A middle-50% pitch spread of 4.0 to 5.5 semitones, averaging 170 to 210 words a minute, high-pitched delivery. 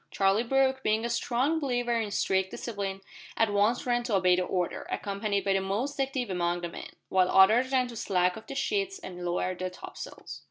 Yes: average, 4.5 semitones; fast, 205 wpm; high, 210 Hz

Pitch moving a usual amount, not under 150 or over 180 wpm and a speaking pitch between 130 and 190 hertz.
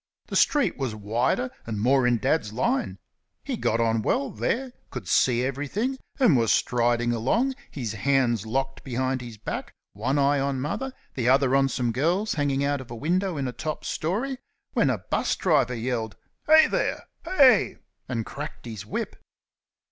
Yes: average, 4.9 semitones; average, 170 wpm; low, 135 Hz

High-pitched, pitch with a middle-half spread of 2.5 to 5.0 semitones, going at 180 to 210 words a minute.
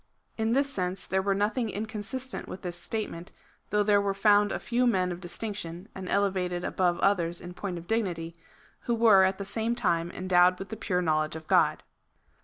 Yes: high, 195 Hz; average, 3.3 semitones; average, 200 wpm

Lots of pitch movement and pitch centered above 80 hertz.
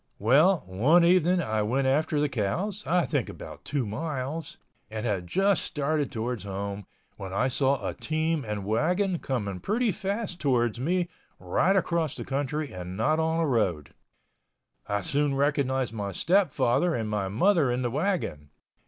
Yes: wide, 7.4 semitones; low, 135 Hz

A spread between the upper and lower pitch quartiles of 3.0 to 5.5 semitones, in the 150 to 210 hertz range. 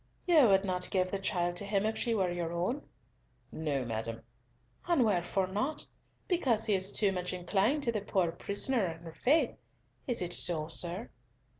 Yes: average, 4.1 semitones; high, 190 Hz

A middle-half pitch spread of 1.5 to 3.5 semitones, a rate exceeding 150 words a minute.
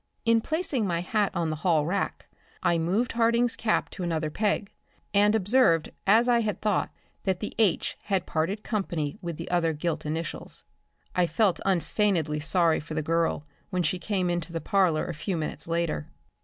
No: average, 4.2 semitones; average, 175 wpm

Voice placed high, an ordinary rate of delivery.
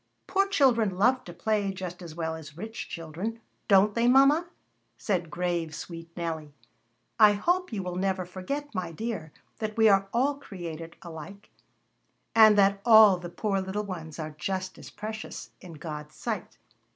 Yes: high, 195 Hz; average, 165 wpm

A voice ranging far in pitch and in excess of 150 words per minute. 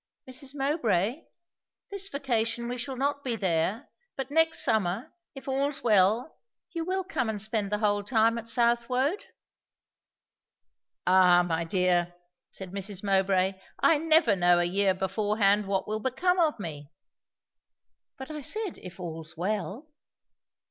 No: wide, 6.2 semitones; average, 140 wpm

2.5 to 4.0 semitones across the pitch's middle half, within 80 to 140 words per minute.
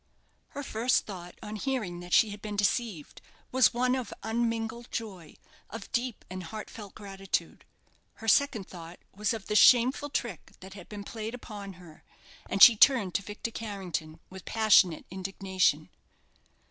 No: average, 3.6 semitones; average, 155 wpm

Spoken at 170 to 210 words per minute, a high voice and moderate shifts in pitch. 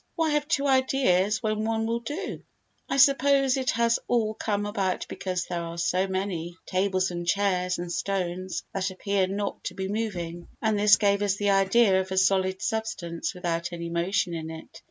Yes: average, 185 wpm; high, 195 Hz; average, 3.5 semitones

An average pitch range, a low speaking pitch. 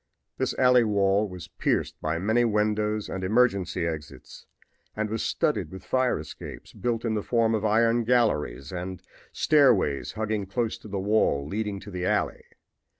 Yes: average, 3.5 semitones; low, 105 Hz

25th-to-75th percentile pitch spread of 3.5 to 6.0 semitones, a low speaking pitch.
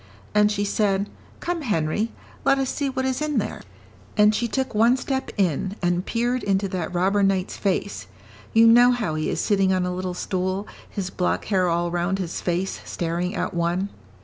No: average, 4.1 semitones; high, 195 Hz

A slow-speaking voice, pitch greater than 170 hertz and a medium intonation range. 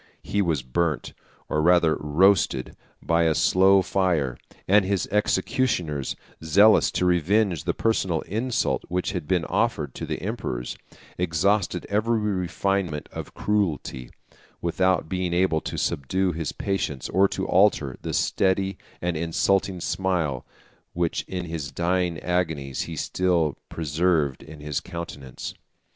No: slow, 130 wpm; very low, 90 Hz; average, 3.6 semitones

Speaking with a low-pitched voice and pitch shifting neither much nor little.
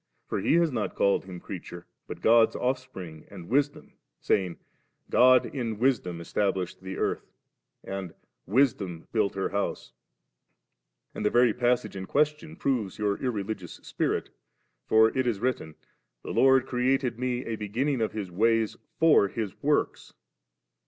Yes: low, 110 Hz; average, 4.8 semitones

